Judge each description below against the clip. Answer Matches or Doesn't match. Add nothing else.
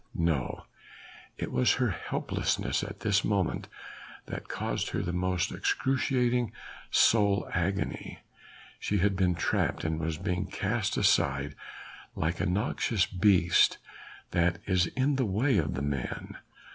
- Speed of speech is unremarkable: Doesn't match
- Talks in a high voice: Doesn't match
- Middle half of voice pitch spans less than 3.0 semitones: Doesn't match